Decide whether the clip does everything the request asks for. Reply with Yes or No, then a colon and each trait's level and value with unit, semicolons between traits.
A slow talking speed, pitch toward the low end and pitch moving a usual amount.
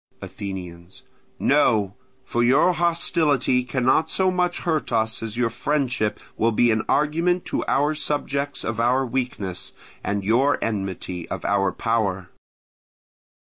No: slow, 130 wpm; low, 120 Hz; wide, 5.9 semitones